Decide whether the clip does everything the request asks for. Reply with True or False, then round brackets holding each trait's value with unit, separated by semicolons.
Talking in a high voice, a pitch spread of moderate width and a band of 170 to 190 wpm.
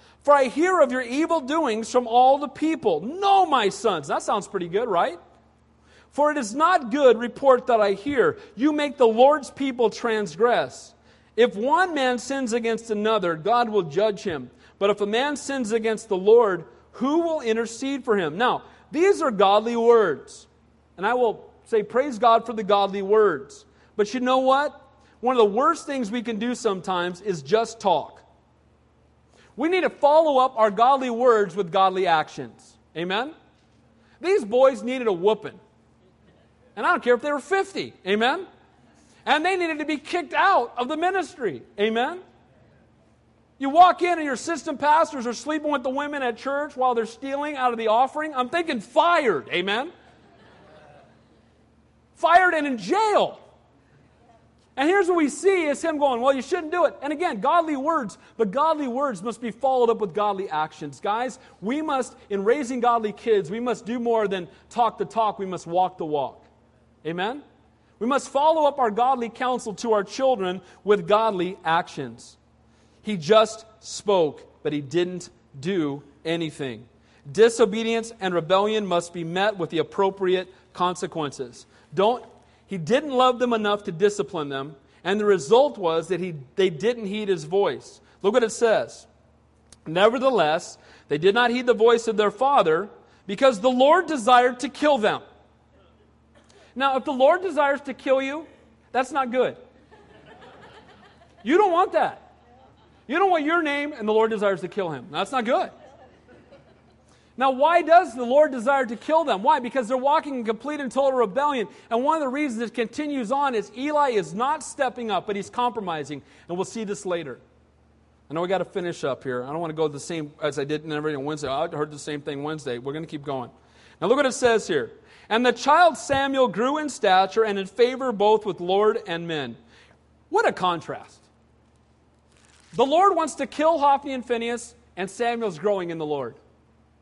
False (235 Hz; 6.4 semitones; 180 wpm)